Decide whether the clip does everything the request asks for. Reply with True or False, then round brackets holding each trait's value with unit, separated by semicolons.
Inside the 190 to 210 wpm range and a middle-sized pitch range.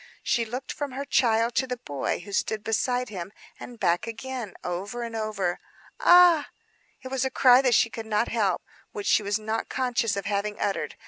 True (195 wpm; 3.5 semitones)